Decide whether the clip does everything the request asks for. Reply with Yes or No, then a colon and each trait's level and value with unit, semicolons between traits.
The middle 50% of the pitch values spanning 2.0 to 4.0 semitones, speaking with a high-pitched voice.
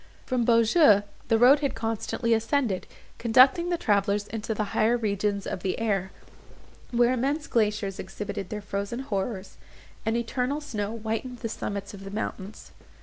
Yes: average, 3.3 semitones; high, 225 Hz